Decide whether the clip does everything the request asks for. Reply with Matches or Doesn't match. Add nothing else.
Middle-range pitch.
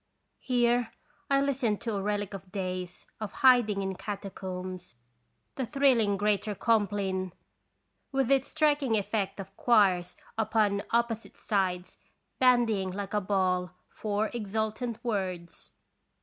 Doesn't match